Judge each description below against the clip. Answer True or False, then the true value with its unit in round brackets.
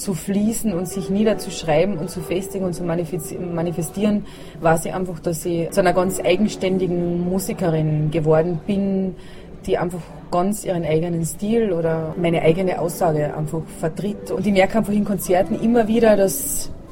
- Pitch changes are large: False (2.9 semitones)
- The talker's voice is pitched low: False (180 Hz)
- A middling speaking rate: True (155 wpm)